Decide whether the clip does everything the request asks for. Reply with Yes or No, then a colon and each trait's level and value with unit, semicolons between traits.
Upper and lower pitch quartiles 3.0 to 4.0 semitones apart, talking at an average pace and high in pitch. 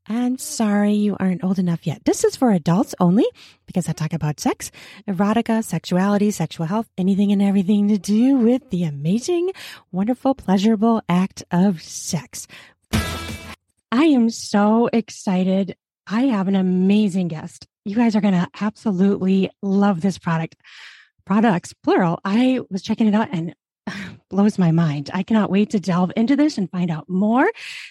Yes: average, 3.6 semitones; average, 160 wpm; high, 200 Hz